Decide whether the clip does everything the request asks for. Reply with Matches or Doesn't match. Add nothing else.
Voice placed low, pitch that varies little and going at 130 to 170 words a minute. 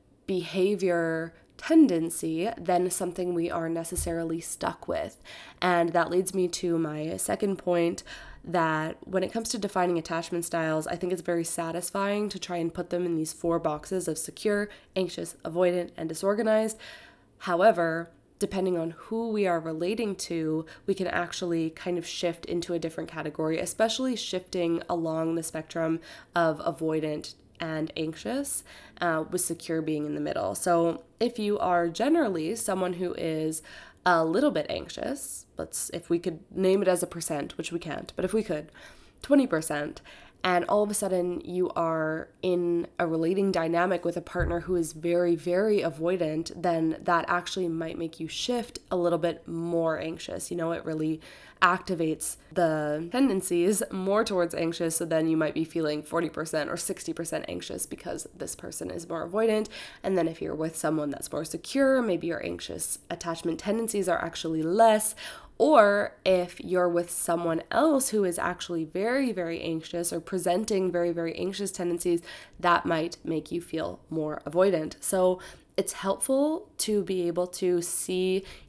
Doesn't match